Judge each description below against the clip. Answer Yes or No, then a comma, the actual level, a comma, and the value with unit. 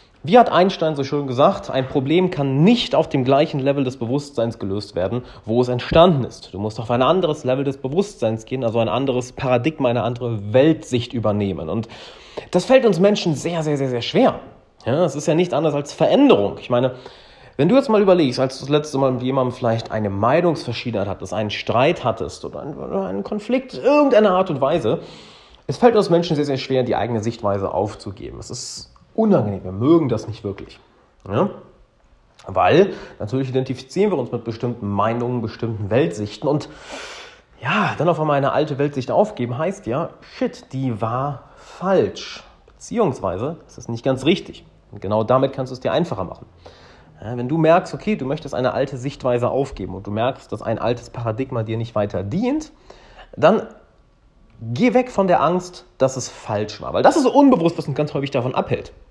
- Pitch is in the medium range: No, low, 130 Hz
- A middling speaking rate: No, fast, 195 wpm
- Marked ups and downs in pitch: Yes, wide, 5.8 semitones